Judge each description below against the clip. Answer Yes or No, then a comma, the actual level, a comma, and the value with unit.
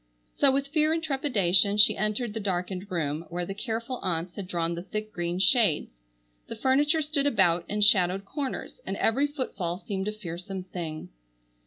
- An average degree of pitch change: No, wide, 6.6 semitones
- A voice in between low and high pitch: No, high, 200 Hz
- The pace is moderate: Yes, average, 175 wpm